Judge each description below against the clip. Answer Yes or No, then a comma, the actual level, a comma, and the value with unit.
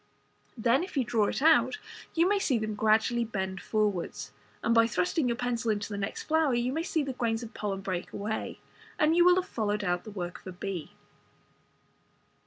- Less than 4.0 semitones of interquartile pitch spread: No, average, 4.6 semitones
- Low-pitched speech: No, high, 225 Hz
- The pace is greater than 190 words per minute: Yes, average, 200 wpm